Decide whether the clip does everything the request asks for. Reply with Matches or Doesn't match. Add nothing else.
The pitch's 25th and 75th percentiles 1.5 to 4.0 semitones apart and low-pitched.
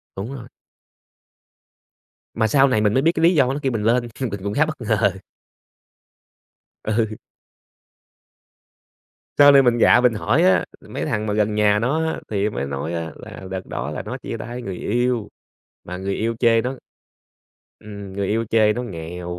Matches